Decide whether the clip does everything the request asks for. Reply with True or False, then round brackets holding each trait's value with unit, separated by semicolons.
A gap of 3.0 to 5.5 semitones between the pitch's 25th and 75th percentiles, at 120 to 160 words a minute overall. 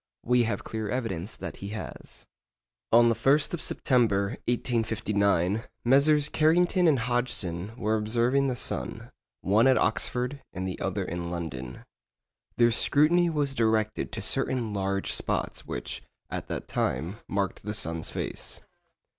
True (4.6 semitones; 140 wpm)